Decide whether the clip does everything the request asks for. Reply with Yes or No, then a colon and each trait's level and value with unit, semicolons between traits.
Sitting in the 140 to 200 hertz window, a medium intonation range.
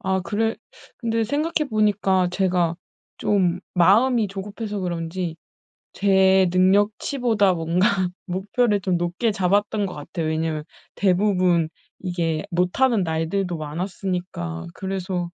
Yes: high, 190 Hz; average, 3.0 semitones